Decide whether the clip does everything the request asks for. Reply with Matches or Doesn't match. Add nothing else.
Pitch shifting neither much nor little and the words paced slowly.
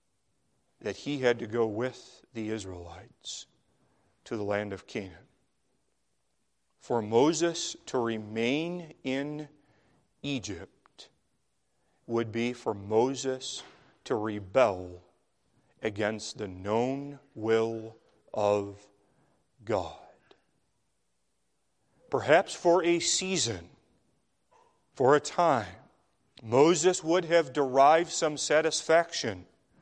Doesn't match